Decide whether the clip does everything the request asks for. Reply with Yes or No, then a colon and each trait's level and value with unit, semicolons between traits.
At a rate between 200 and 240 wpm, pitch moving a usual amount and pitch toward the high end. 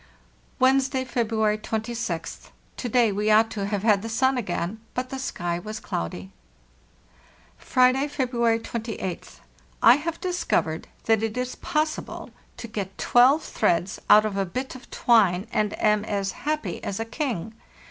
No: average, 150 wpm; average, 4.1 semitones; high, 225 Hz